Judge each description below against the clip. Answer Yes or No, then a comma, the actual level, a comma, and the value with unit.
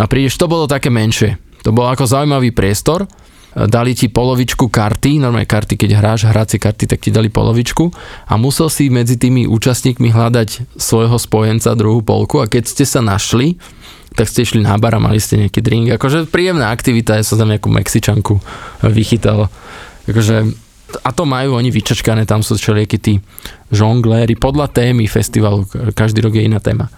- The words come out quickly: Yes, fast, 175 wpm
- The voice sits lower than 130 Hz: Yes, low, 115 Hz